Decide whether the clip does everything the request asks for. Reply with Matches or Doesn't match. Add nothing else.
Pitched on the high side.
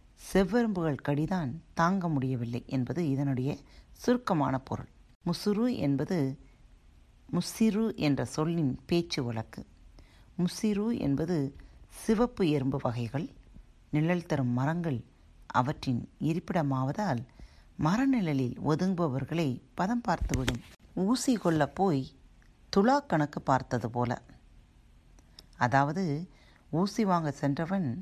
Doesn't match